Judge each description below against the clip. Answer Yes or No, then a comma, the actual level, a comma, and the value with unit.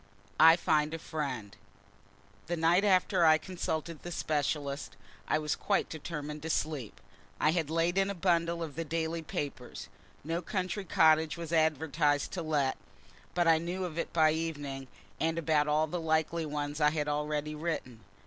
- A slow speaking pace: No, average, 170 wpm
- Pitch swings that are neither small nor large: No, narrow, 2.1 semitones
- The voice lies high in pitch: No, medium, 160 Hz